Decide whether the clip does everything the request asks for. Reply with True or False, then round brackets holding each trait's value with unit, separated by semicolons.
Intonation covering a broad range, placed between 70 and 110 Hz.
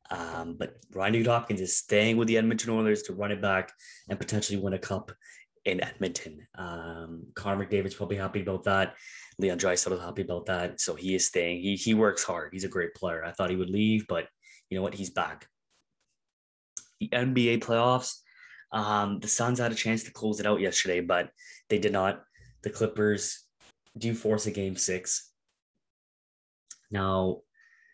False (2.9 semitones; 105 Hz)